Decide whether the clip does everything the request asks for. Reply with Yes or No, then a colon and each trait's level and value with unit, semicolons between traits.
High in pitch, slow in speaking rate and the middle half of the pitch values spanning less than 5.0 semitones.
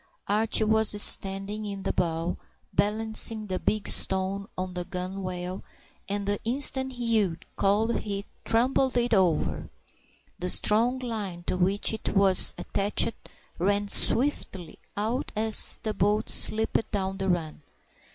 Yes: high, 205 Hz; slow, 130 wpm; average, 2.8 semitones